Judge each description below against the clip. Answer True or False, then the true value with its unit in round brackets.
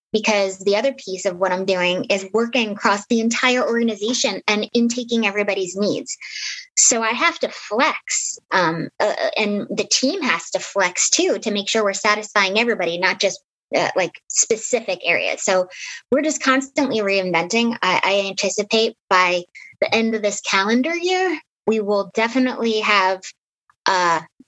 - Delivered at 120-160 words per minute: True (155 wpm)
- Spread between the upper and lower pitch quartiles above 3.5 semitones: True (4.3 semitones)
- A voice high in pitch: True (215 Hz)